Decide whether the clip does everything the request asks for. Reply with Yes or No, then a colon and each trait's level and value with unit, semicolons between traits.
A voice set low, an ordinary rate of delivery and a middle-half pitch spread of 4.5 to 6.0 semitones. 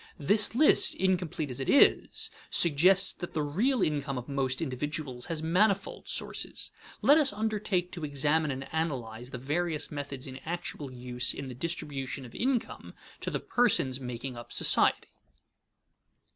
No: medium, 150 Hz; average, 150 wpm; wide, 5.4 semitones